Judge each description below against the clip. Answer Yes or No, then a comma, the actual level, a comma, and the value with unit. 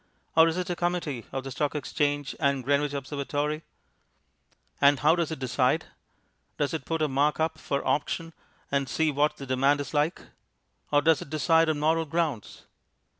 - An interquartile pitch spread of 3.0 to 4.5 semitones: No, narrow, 2.5 semitones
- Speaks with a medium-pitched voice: Yes, medium, 145 Hz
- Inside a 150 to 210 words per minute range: Yes, average, 175 wpm